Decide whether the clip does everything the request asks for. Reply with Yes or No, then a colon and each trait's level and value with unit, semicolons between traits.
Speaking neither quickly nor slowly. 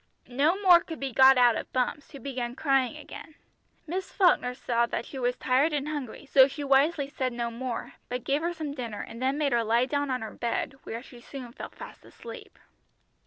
No: fast, 210 wpm